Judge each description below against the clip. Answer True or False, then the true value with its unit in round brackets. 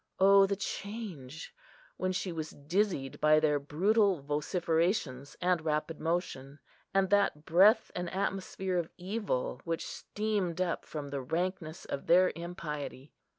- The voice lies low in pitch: False (170 Hz)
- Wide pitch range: False (4.2 semitones)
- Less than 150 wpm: True (135 wpm)